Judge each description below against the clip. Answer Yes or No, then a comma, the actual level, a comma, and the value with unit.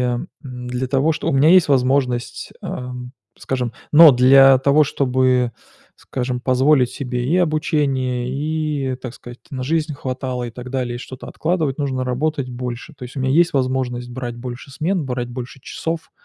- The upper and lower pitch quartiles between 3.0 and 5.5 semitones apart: No, narrow, 2.6 semitones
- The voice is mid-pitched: No, low, 130 Hz